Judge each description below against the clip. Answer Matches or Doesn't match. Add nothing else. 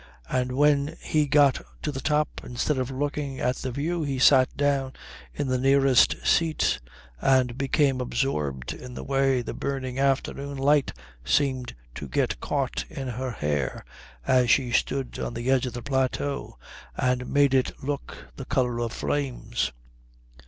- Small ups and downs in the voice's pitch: Matches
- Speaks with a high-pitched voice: Doesn't match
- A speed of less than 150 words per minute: Doesn't match